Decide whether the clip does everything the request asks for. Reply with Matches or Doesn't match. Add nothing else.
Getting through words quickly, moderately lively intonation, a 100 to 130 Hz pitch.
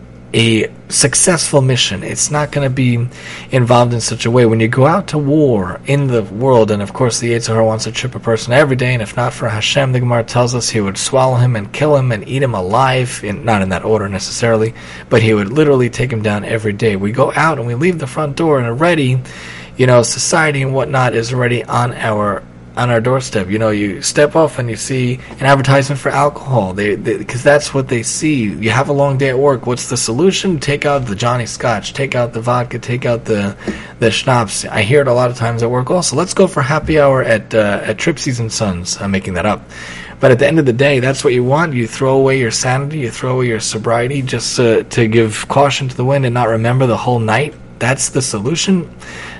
Matches